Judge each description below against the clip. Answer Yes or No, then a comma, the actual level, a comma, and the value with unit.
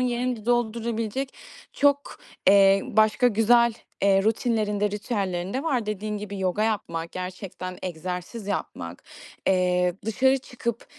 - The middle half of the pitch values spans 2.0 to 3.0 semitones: No, average, 4.0 semitones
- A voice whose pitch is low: No, high, 210 Hz